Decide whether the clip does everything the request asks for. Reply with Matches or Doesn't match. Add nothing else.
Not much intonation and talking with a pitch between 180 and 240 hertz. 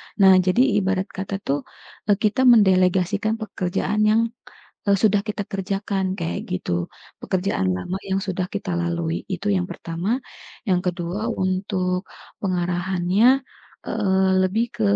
Matches